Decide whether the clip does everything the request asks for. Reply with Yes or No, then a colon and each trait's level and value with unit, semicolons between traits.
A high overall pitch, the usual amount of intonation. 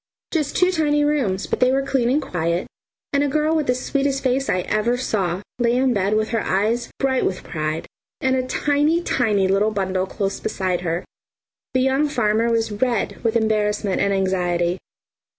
No: high, 230 Hz; wide, 5.8 semitones